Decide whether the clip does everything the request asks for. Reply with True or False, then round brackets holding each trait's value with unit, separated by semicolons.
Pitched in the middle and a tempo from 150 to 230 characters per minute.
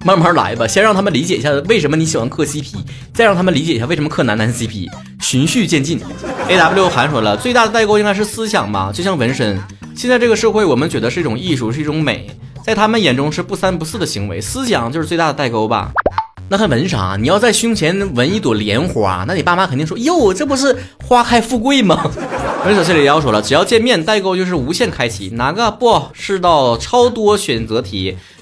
False (160 Hz; 340 characters per minute)